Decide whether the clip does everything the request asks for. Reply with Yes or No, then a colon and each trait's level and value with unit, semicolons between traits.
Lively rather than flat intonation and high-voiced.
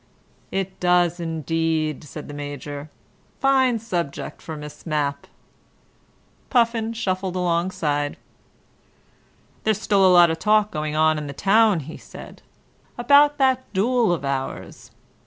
No: wide, 6.2 semitones; medium, 175 Hz